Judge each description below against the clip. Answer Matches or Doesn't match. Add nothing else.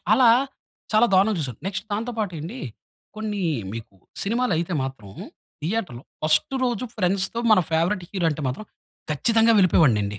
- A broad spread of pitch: Matches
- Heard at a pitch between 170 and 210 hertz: Matches